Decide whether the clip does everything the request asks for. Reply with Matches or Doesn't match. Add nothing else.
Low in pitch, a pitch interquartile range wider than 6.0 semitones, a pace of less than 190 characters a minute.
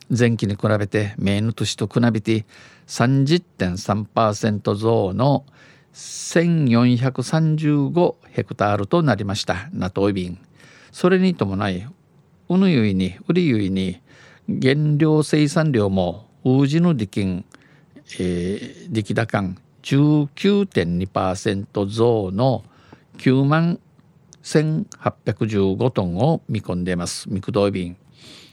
Matches